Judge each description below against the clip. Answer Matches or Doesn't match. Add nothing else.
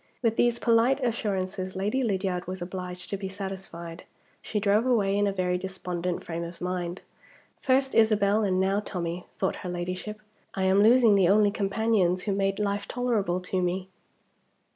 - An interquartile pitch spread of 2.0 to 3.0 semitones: Matches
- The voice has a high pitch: Matches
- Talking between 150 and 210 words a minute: Matches